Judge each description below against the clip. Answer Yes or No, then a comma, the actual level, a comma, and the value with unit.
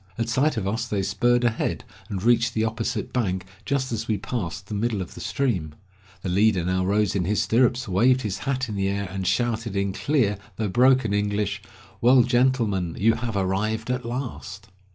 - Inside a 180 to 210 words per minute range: Yes, average, 195 wpm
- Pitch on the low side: Yes, low, 110 Hz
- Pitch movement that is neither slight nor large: Yes, average, 3.7 semitones